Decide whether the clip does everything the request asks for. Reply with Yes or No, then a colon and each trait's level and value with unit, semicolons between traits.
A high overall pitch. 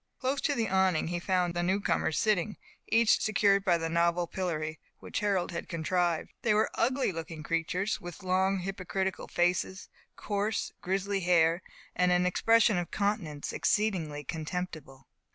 No: medium, 180 Hz